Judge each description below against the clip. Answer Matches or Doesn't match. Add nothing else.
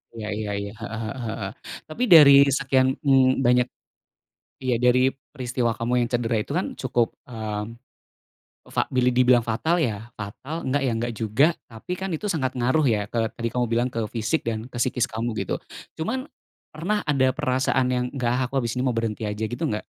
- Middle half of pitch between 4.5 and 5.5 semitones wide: Doesn't match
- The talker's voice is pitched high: Doesn't match